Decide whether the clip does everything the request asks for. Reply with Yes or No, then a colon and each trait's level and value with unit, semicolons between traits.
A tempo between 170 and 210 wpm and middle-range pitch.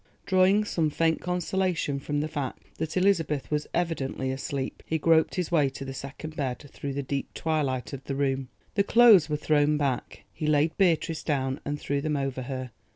Yes: average, 190 wpm; medium, 150 Hz